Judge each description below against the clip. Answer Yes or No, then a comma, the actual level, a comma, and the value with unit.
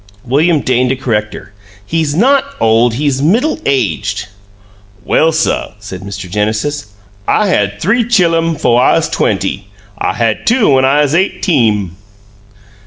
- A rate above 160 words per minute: No, average, 145 wpm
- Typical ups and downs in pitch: No, wide, 7.5 semitones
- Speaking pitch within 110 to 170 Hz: Yes, low, 135 Hz